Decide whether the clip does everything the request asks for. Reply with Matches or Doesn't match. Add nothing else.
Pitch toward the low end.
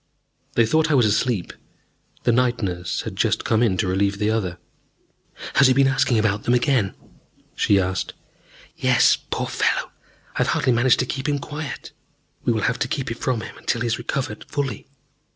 Matches